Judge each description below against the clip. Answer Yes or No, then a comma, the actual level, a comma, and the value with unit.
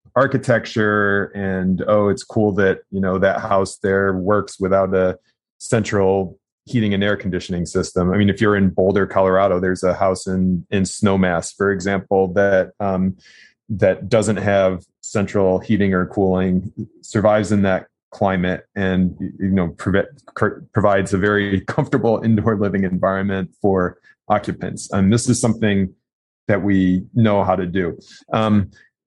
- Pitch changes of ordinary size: No, narrow, 1.7 semitones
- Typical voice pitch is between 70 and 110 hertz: Yes, very low, 95 Hz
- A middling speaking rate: Yes, average, 150 wpm